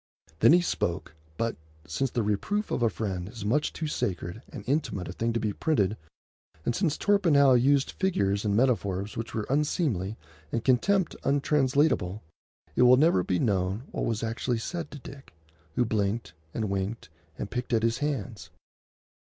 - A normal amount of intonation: No, wide, 5.7 semitones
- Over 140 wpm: Yes, average, 170 wpm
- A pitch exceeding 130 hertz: No, low, 115 Hz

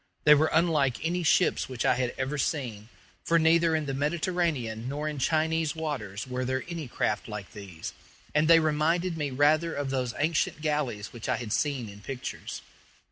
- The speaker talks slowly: No, average, 185 wpm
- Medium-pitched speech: Yes, medium, 145 Hz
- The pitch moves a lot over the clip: No, average, 4.3 semitones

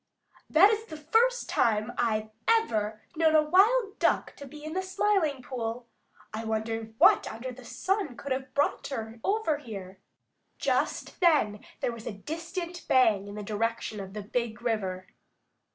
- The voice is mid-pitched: No, very high, 250 Hz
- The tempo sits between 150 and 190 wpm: Yes, average, 165 wpm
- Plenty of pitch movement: Yes, wide, 7.2 semitones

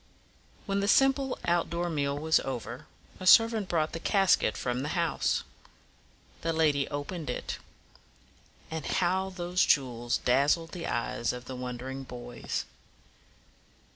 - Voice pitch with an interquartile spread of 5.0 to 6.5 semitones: Yes, wide, 5.5 semitones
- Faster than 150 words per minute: No, slow, 135 wpm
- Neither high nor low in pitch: Yes, medium, 160 Hz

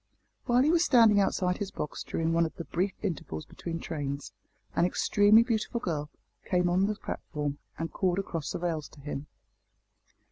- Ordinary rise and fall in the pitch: Yes, average, 4.8 semitones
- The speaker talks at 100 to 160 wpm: No, average, 175 wpm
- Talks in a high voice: No, medium, 175 Hz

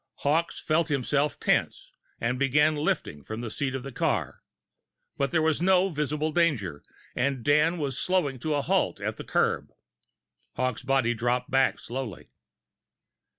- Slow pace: No, average, 150 wpm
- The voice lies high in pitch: No, medium, 140 Hz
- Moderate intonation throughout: Yes, average, 3.6 semitones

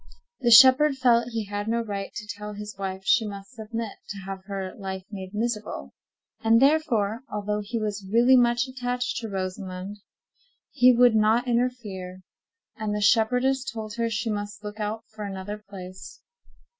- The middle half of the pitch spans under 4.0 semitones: Yes, average, 3.0 semitones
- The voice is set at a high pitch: Yes, high, 215 Hz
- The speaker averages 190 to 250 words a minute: No, average, 165 wpm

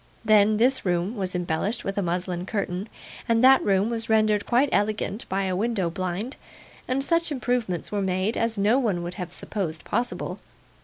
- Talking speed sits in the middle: Yes, average, 175 wpm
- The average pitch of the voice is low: No, high, 205 Hz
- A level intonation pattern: No, average, 3.9 semitones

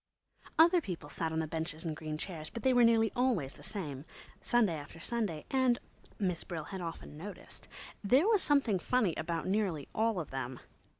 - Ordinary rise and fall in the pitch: No, wide, 6.7 semitones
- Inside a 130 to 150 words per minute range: No, average, 175 wpm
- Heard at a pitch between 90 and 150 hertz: No, medium, 185 Hz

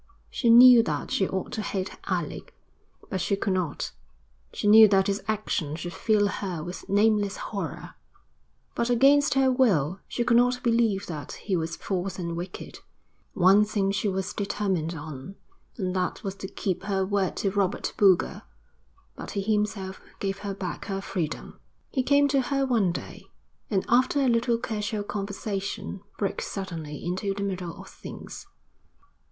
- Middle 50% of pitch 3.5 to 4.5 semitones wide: No, average, 3.0 semitones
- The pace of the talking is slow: No, average, 165 wpm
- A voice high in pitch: Yes, high, 200 Hz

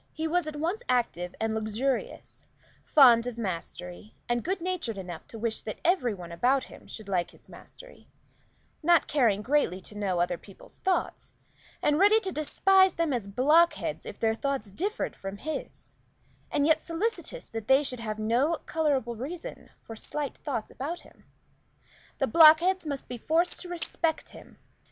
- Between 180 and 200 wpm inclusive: No, average, 165 wpm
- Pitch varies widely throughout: Yes, wide, 7.1 semitones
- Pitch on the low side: No, very high, 270 Hz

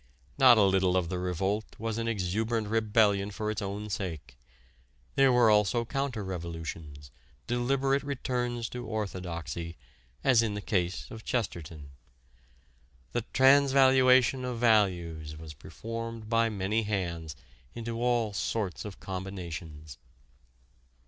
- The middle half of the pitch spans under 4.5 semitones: No, average, 4.8 semitones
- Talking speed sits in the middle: No, slow, 120 wpm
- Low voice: Yes, low, 105 Hz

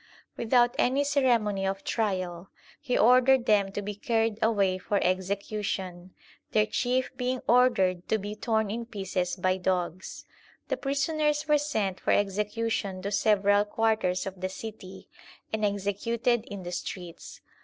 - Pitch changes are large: No, average, 3.9 semitones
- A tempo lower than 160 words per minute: Yes, average, 145 wpm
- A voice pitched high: Yes, high, 210 Hz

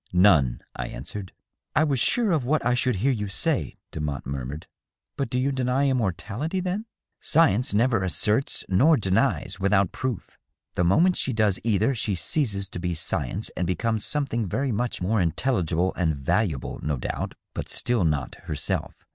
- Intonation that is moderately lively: No, wide, 6.7 semitones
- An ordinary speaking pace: Yes, average, 180 wpm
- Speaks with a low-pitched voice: Yes, low, 105 Hz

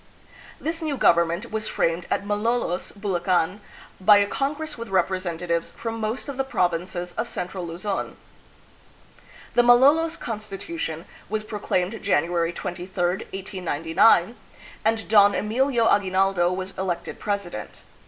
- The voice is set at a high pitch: Yes, high, 195 Hz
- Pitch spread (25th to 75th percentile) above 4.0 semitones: Yes, average, 4.4 semitones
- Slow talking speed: Yes, slow, 125 wpm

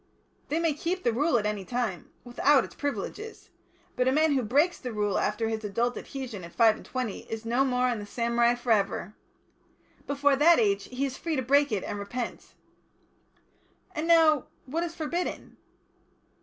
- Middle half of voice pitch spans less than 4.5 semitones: No, average, 4.8 semitones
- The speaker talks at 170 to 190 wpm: Yes, average, 185 wpm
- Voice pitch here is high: Yes, very high, 250 Hz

